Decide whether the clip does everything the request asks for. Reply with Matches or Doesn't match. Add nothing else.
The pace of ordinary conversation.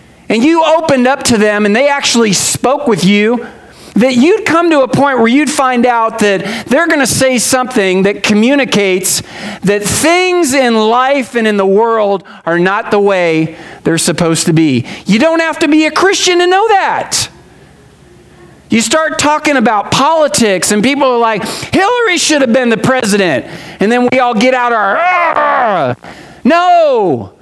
Matches